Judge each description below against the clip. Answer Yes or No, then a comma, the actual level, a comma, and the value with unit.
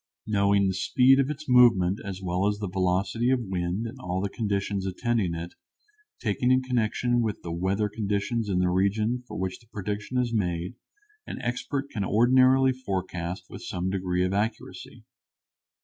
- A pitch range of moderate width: Yes, average, 4.4 semitones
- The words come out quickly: No, average, 170 wpm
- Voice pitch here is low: Yes, low, 100 Hz